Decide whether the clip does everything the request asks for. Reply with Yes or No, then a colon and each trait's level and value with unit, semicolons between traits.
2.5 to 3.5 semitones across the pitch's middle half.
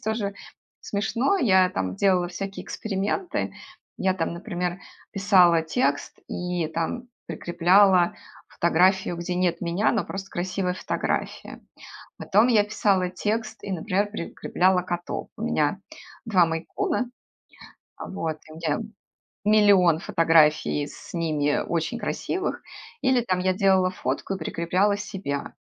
Yes: average, 3.2 semitones